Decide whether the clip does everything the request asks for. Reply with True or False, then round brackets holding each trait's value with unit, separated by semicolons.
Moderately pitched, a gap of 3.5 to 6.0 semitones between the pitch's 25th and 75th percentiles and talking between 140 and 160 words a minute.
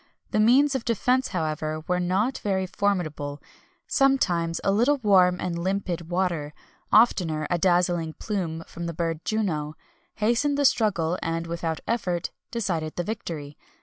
True (180 Hz; 4.5 semitones; 150 wpm)